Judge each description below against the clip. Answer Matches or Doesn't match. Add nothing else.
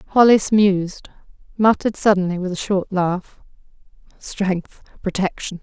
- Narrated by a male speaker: Doesn't match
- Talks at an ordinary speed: Doesn't match